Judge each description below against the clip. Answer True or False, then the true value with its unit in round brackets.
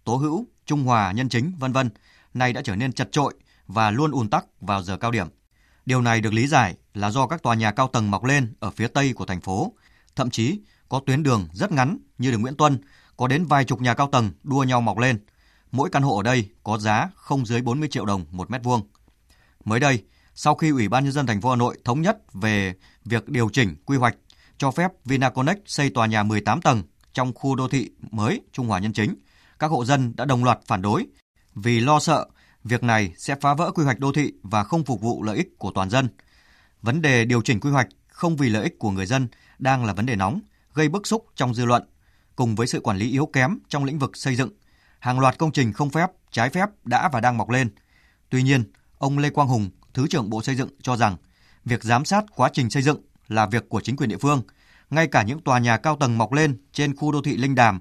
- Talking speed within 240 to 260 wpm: True (245 wpm)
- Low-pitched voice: True (125 Hz)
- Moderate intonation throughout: True (4.5 semitones)